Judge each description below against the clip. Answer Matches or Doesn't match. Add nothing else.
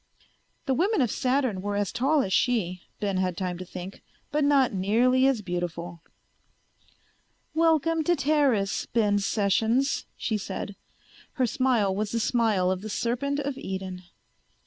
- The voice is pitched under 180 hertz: Doesn't match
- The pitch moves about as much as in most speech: Doesn't match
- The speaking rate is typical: Matches